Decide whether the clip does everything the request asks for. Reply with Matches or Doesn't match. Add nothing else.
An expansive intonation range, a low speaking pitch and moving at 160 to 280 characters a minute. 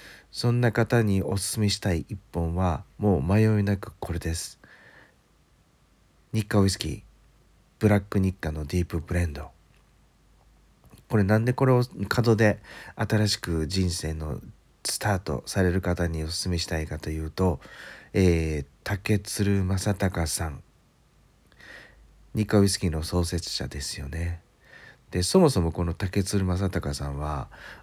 Doesn't match